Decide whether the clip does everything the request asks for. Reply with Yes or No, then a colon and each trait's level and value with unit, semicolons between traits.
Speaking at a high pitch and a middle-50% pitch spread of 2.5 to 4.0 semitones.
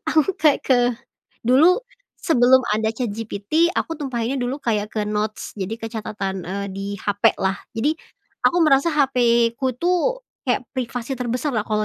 No: high, 245 Hz; average, 4.8 semitones